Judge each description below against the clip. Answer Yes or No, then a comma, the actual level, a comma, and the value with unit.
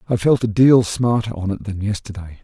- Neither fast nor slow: No, fast, 220 wpm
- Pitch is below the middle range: Yes, low, 105 Hz